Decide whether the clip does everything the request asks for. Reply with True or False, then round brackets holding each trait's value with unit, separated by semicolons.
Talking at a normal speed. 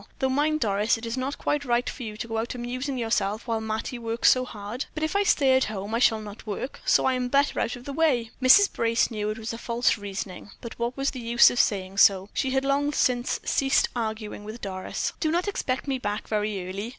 False (240 wpm)